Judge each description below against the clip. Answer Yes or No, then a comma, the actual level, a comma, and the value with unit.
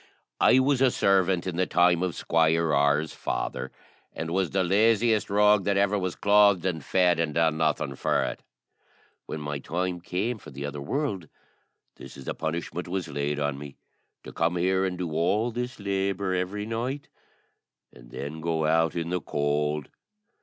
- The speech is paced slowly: No, average, 175 wpm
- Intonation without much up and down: No, average, 4.2 semitones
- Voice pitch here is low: Yes, very low, 90 Hz